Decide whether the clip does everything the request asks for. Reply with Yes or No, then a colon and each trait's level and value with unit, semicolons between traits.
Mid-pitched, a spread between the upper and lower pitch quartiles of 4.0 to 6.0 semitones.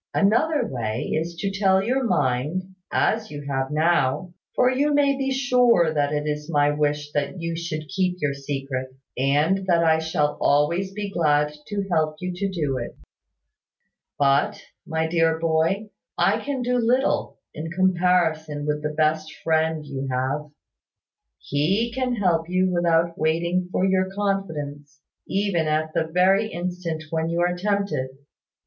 Yes: medium, 165 Hz; average, 4.5 semitones